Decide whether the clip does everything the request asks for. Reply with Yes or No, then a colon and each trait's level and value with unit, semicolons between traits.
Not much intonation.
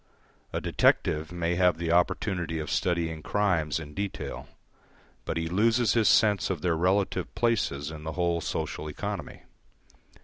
No: average, 3.7 semitones